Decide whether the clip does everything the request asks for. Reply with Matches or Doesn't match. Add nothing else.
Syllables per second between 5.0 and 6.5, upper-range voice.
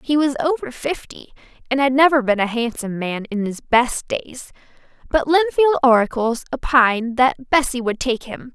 Matches